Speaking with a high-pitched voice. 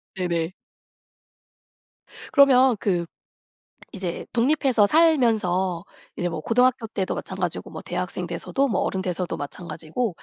Yes: high, 195 Hz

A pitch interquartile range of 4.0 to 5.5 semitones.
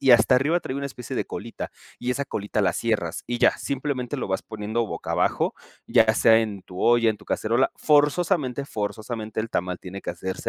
Yes: average, 4.3 semitones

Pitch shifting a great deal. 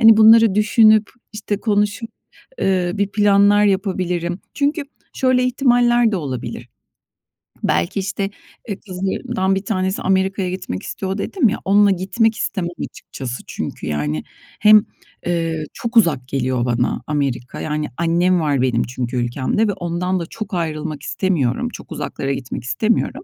Yes: wide, 5.9 semitones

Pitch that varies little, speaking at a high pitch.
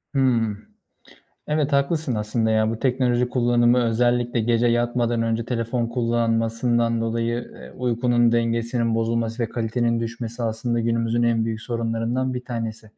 No: narrow, 1.1 semitones; low, 115 Hz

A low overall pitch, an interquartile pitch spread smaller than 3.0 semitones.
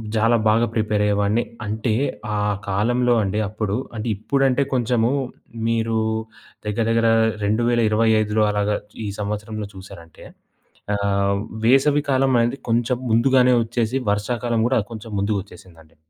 Yes: low, 110 Hz; narrow, 2.6 semitones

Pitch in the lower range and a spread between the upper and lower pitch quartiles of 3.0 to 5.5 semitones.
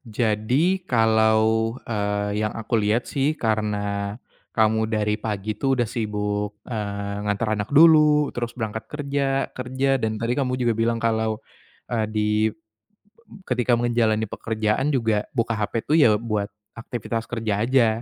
No: low, 110 Hz; narrow, 2.5 semitones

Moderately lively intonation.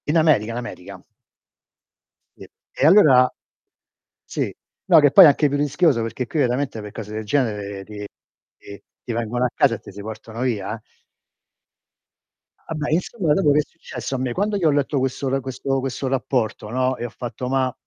Yes: average, 4.3 semitones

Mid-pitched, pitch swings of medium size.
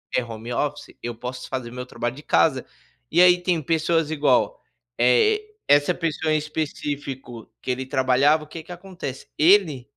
Yes: medium, 145 Hz; average, 4.2 semitones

